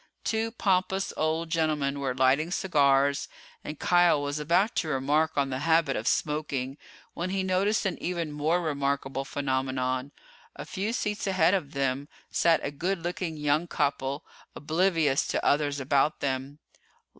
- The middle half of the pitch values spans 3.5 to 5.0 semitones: Yes, average, 4.0 semitones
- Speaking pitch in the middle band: Yes, medium, 150 Hz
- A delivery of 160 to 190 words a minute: No, average, 150 wpm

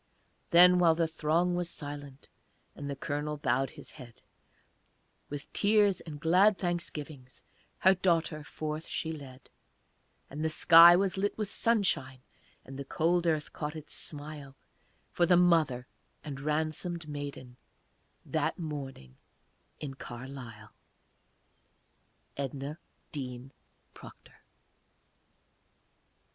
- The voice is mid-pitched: Yes, medium, 150 Hz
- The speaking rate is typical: No, slow, 110 wpm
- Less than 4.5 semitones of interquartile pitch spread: Yes, average, 3.9 semitones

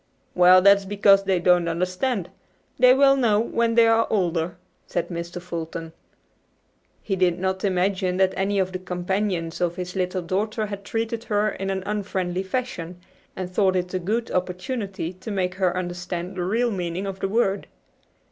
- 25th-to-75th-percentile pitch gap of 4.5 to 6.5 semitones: No, narrow, 2.4 semitones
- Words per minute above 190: No, average, 175 wpm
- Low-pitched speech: No, high, 190 Hz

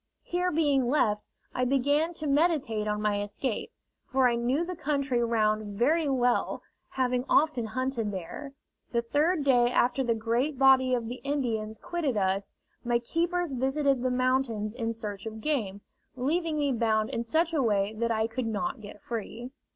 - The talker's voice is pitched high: Yes, very high, 250 Hz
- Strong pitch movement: No, average, 4.3 semitones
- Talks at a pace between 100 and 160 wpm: No, average, 170 wpm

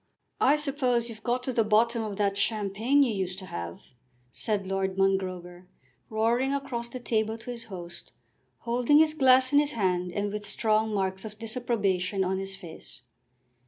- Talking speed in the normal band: Yes, average, 170 wpm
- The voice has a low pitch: No, high, 215 Hz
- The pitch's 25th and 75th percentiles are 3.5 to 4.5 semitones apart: Yes, average, 4.0 semitones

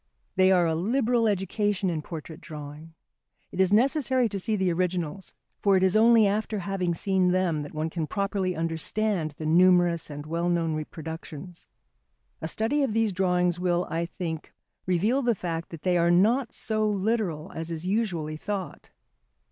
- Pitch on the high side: No, medium, 180 Hz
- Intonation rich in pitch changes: No, average, 3.9 semitones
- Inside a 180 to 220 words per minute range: No, average, 170 wpm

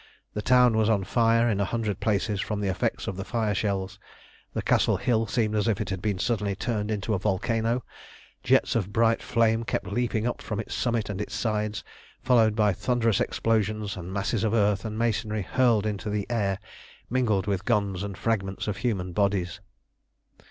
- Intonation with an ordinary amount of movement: No, narrow, 2.3 semitones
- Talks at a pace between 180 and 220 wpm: Yes, average, 185 wpm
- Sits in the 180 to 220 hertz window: No, low, 105 Hz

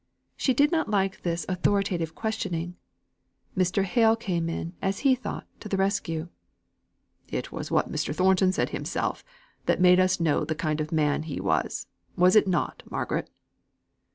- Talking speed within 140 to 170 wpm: Yes, average, 160 wpm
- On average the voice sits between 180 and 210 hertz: Yes, medium, 185 Hz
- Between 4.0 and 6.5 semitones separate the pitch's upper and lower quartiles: No, average, 3.2 semitones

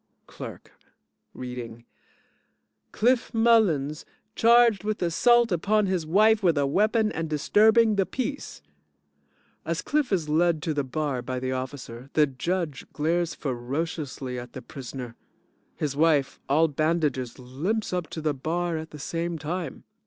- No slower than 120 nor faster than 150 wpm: Yes, average, 140 wpm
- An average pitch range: No, wide, 6.3 semitones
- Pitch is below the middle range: No, medium, 160 Hz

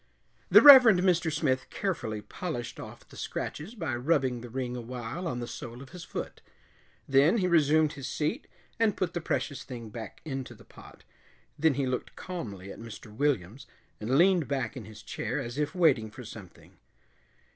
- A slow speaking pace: No, average, 180 wpm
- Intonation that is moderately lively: No, wide, 5.7 semitones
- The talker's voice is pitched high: No, low, 135 Hz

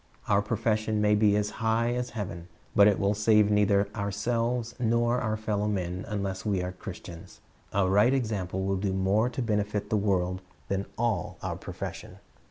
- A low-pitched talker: Yes, low, 105 Hz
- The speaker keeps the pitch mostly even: Yes, narrow, 2.3 semitones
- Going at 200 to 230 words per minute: No, average, 175 wpm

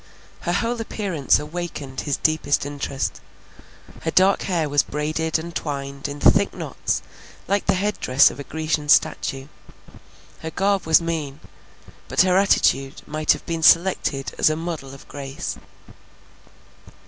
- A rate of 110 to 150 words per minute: Yes, average, 145 wpm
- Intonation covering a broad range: No, average, 3.5 semitones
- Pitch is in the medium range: Yes, medium, 155 Hz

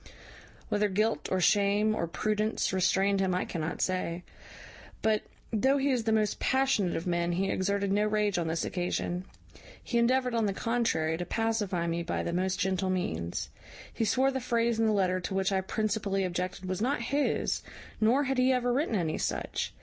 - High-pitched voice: Yes, high, 200 Hz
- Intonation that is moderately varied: Yes, average, 3.7 semitones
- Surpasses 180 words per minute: Yes, average, 190 wpm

